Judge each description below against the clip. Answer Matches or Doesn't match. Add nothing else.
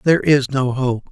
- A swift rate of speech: Matches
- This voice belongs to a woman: Doesn't match